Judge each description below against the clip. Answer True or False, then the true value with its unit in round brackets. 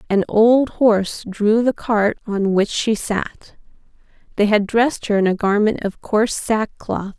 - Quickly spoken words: False (165 wpm)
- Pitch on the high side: True (215 Hz)